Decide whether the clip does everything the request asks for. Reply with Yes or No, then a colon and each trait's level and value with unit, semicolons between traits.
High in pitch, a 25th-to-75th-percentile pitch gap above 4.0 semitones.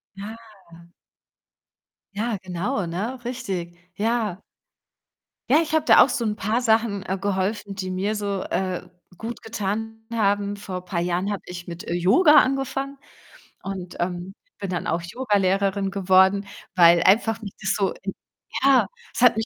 No: high, 200 Hz; average, 3.2 semitones